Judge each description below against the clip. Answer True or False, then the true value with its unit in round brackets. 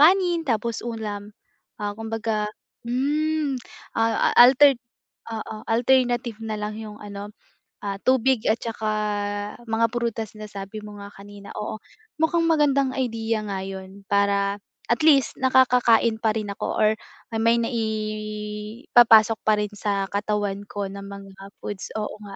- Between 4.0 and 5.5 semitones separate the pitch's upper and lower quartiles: False (2.7 semitones)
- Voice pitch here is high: True (220 Hz)